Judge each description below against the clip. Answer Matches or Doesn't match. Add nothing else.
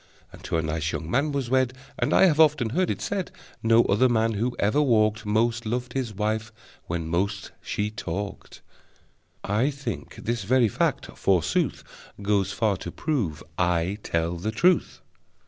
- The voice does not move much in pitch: Doesn't match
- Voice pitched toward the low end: Matches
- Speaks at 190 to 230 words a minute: Doesn't match